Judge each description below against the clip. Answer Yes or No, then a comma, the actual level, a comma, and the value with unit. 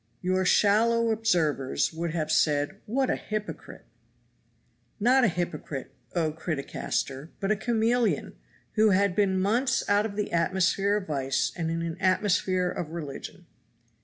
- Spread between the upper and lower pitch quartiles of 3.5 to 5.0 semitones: Yes, average, 4.7 semitones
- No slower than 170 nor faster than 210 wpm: No, average, 140 wpm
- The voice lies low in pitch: No, medium, 185 Hz